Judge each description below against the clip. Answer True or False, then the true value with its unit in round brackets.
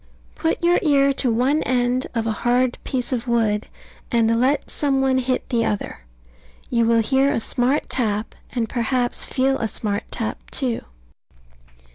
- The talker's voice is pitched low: False (245 Hz)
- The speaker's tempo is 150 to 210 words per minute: True (160 wpm)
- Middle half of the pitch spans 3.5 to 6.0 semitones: False (2.7 semitones)